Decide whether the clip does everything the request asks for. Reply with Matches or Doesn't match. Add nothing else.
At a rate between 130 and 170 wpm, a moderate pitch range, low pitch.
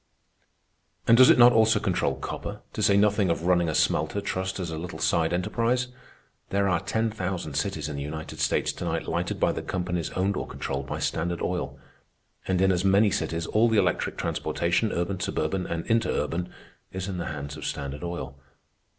Doesn't match